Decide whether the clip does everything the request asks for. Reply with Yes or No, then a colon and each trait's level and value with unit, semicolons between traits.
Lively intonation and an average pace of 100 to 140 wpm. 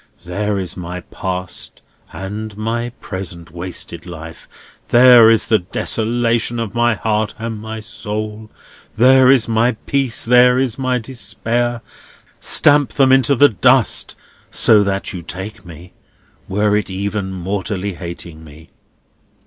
No: average, 4.1 semitones; slow, 135 wpm